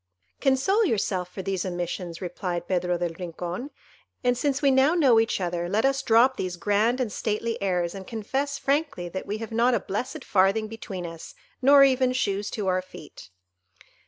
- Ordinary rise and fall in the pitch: No, wide, 6.1 semitones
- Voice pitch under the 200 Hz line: No, high, 210 Hz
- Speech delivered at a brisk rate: No, average, 180 wpm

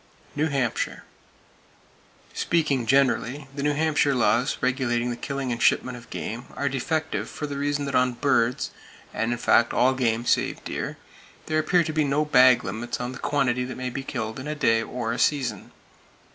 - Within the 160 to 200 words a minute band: Yes, average, 185 wpm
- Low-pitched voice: Yes, low, 130 Hz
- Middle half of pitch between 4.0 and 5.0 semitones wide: No, average, 3.1 semitones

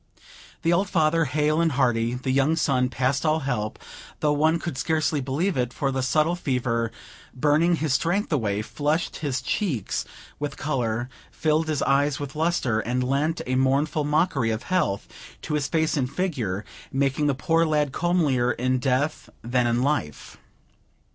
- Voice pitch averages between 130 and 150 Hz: Yes, medium, 140 Hz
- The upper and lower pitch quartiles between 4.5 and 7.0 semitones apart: No, average, 3.8 semitones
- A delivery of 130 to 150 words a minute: No, average, 160 wpm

